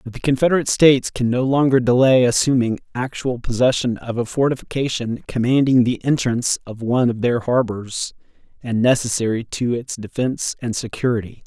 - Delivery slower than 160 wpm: Yes, average, 150 wpm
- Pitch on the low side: Yes, low, 125 Hz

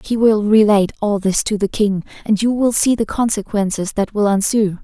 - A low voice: No, high, 210 Hz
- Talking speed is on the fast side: Yes, fast, 210 wpm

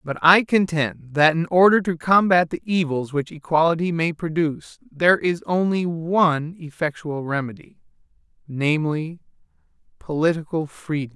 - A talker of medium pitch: Yes, medium, 160 Hz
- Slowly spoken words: Yes, slow, 120 wpm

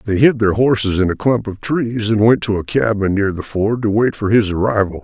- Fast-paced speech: Yes, fast, 260 wpm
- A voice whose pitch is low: Yes, low, 105 Hz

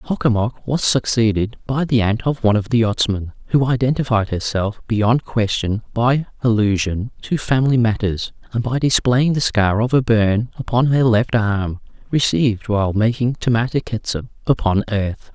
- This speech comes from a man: Yes, male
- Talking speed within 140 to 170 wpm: Yes, average, 165 wpm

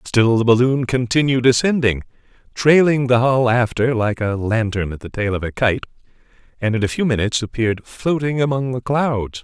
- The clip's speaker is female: No, male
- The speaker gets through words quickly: No, average, 180 wpm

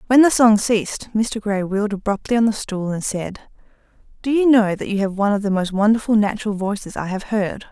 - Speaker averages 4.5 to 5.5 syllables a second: No, 5.8 syllables/s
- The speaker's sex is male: No, female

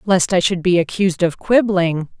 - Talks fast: No, average, 190 wpm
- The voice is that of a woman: Yes, female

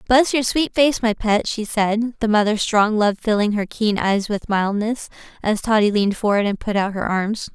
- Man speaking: No, female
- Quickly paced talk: Yes, fast, 215 wpm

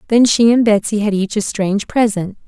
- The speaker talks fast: Yes, fast, 220 wpm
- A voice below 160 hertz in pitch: No, high, 210 Hz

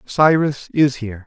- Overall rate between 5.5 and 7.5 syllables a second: No, 4.5 syllables/s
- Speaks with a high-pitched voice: No, medium, 140 Hz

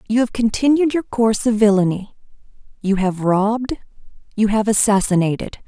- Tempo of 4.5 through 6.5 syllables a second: Yes, 5.3 syllables/s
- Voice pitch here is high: Yes, high, 215 Hz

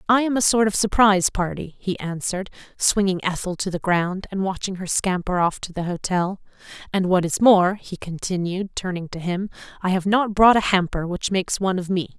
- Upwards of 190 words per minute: Yes, fast, 205 wpm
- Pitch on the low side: No, high, 190 Hz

